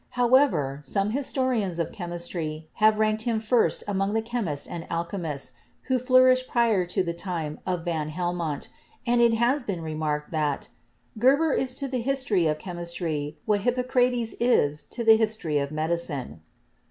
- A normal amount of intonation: No, wide, 7.0 semitones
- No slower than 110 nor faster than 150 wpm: No, average, 160 wpm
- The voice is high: Yes, high, 195 Hz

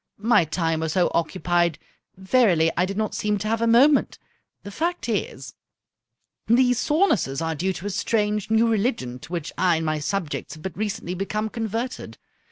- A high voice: Yes, high, 195 Hz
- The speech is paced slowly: No, average, 175 wpm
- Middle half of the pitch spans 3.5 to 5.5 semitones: Yes, average, 5.1 semitones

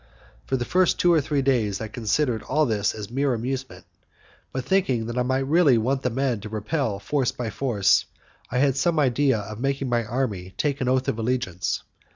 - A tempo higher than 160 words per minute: Yes, average, 200 wpm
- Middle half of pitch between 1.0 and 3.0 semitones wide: No, average, 3.8 semitones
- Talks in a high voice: No, low, 125 Hz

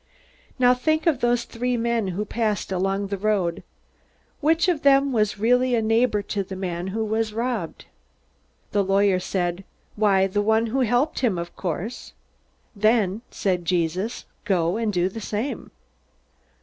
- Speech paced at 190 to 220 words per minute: No, average, 155 wpm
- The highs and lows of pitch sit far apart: No, average, 4.0 semitones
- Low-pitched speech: No, high, 215 Hz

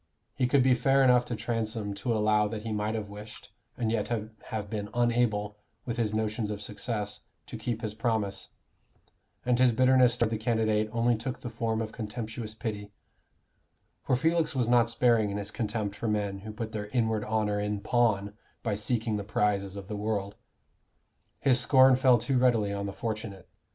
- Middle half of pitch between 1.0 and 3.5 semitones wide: Yes, narrow, 2.5 semitones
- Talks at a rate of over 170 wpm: Yes, average, 185 wpm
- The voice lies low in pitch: Yes, low, 110 Hz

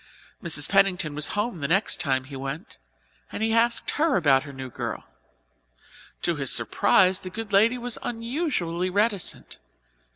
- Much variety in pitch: Yes, wide, 7.2 semitones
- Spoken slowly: No, average, 155 wpm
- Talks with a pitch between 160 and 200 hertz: Yes, medium, 185 Hz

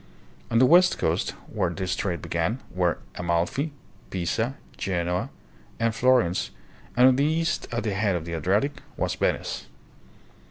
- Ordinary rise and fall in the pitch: No, wide, 6.7 semitones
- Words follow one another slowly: No, average, 150 wpm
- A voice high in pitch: No, low, 100 Hz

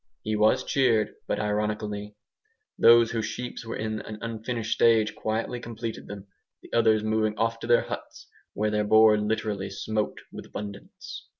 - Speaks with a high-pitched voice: No, low, 110 Hz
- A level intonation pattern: Yes, narrow, 1.4 semitones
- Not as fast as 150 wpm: No, average, 160 wpm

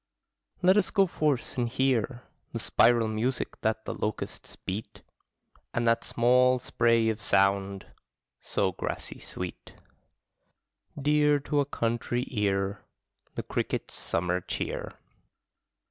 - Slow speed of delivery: Yes, slow, 115 wpm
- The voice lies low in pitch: Yes, low, 115 Hz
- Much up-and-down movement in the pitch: No, average, 3.9 semitones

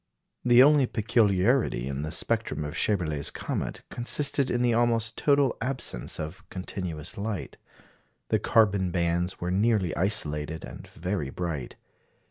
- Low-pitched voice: Yes, very low, 95 Hz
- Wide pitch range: Yes, wide, 6.4 semitones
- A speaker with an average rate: No, slow, 130 wpm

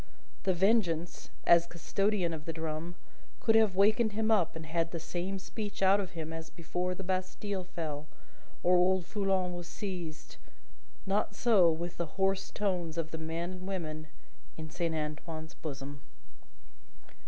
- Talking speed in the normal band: Yes, average, 155 wpm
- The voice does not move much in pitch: No, average, 3.1 semitones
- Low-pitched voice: No, medium, 175 Hz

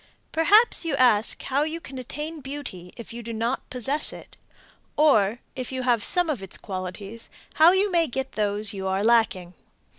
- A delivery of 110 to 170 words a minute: No, average, 180 wpm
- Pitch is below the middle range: No, very high, 250 Hz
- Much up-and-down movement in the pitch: Yes, wide, 6.3 semitones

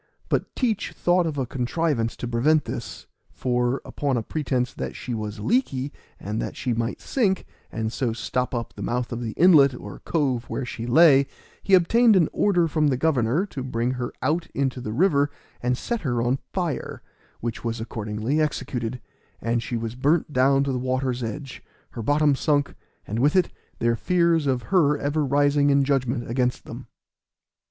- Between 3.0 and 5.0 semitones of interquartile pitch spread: Yes, average, 4.2 semitones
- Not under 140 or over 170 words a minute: No, average, 180 wpm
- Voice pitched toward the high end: No, low, 135 Hz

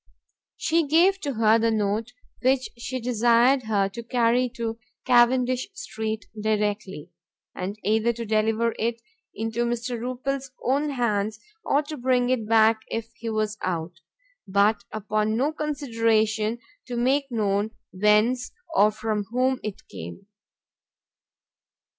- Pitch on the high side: Yes, high, 230 Hz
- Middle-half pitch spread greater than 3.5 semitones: No, average, 2.8 semitones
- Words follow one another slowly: Yes, slow, 130 wpm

